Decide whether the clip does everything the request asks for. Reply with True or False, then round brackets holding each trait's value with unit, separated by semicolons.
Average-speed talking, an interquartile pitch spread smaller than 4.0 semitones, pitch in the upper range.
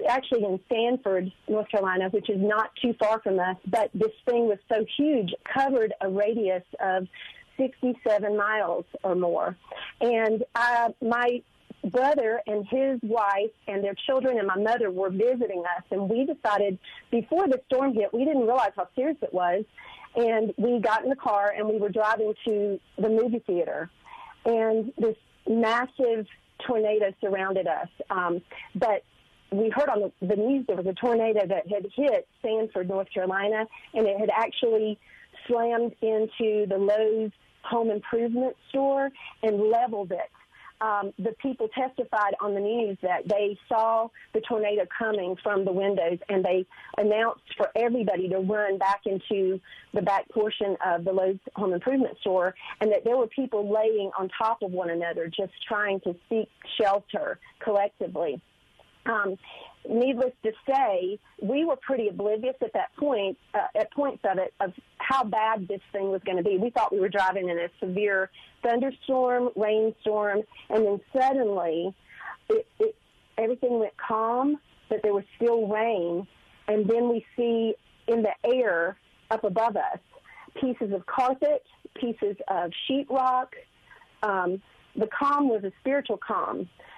True (160 wpm; 3.4 semitones; 220 Hz)